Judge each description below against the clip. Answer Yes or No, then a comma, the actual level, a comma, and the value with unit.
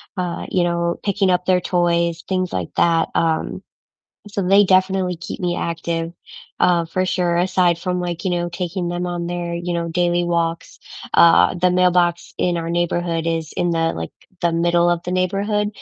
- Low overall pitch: No, medium, 175 Hz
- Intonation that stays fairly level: Yes, narrow, 1.1 semitones